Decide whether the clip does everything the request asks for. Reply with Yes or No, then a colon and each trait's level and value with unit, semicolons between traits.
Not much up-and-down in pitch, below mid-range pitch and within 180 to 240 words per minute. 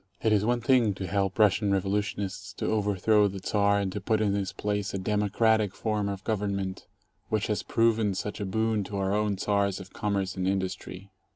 Yes: narrow, 1.6 semitones; low, 100 Hz; average, 195 wpm